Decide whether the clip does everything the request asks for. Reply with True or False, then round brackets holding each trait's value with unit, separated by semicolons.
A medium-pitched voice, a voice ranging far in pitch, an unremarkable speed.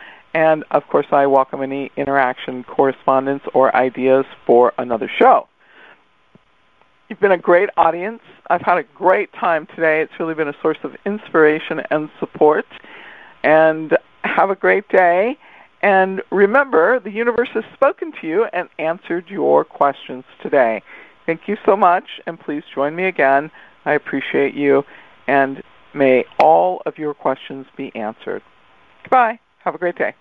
True (160 Hz; 6.1 semitones; 150 wpm)